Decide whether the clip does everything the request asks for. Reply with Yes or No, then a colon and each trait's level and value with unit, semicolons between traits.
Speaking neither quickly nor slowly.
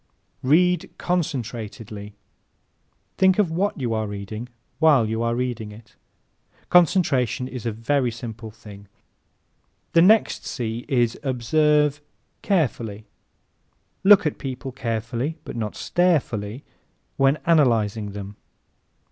No: slow, 115 wpm